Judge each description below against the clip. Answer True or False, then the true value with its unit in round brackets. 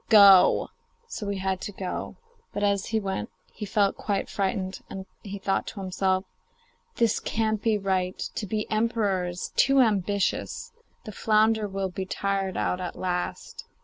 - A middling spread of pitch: False (2.0 semitones)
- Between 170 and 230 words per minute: False (160 wpm)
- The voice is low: False (200 Hz)